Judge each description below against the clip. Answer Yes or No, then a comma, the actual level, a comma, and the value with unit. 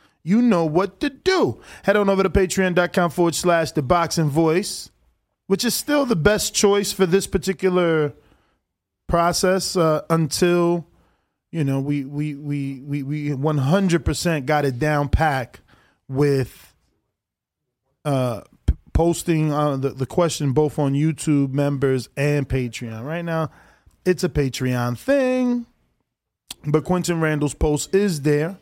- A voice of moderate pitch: Yes, medium, 160 Hz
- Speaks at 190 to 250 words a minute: No, slow, 135 wpm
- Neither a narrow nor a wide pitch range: Yes, average, 4.5 semitones